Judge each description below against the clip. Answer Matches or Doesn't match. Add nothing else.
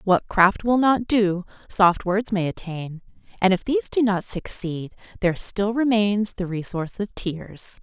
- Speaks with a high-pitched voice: Matches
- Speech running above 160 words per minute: Matches